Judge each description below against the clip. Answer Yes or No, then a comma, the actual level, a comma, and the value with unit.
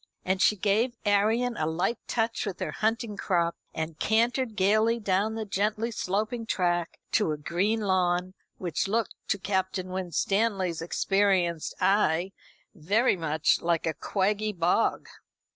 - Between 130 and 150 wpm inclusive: Yes, average, 140 wpm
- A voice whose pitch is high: Yes, high, 195 Hz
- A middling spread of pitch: Yes, average, 3.7 semitones